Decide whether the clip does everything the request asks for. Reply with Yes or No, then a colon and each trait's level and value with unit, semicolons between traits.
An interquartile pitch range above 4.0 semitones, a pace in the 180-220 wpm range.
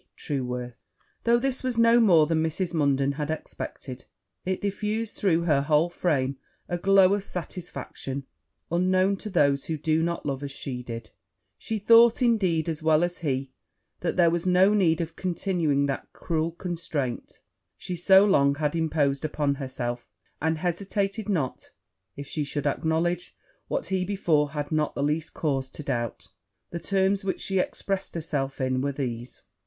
No: average, 4.9 semitones; average, 165 wpm